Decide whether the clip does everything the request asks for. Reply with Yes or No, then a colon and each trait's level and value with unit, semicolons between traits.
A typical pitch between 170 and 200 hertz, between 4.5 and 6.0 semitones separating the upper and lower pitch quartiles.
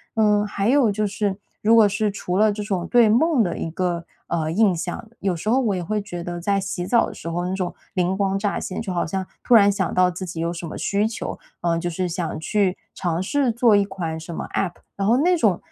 No: high, 195 Hz; average, 3.3 semitones